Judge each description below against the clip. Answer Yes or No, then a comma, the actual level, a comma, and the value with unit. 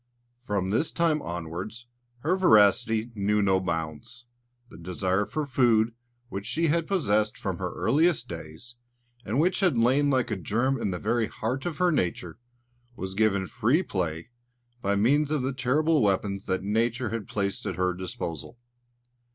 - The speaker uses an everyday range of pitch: No, wide, 6.0 semitones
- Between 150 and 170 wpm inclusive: Yes, average, 160 wpm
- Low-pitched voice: Yes, low, 110 Hz